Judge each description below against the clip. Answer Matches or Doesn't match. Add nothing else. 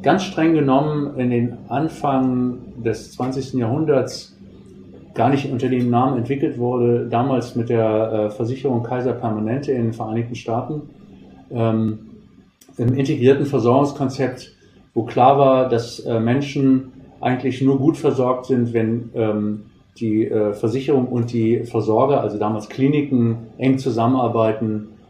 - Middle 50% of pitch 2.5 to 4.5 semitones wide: Matches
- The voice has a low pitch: Matches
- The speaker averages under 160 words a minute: Matches